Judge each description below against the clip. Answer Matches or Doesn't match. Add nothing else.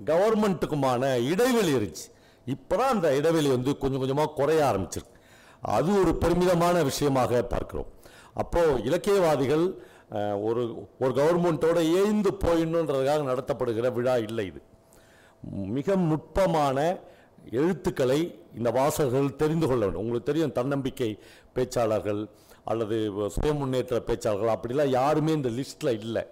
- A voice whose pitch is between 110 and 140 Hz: Matches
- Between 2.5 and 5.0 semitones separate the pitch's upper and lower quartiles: Doesn't match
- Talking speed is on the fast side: Doesn't match